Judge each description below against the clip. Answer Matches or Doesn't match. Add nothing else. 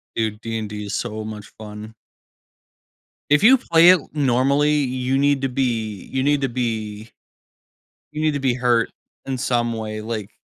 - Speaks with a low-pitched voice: Matches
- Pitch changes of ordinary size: Matches